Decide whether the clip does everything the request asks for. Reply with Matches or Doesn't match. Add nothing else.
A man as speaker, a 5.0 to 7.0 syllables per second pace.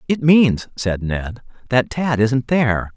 Doesn't match